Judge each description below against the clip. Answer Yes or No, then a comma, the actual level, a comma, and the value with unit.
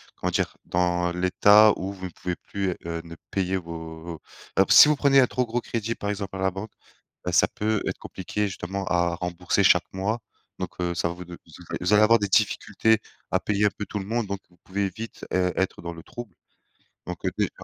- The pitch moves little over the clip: No, average, 3.1 semitones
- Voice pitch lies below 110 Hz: Yes, very low, 95 Hz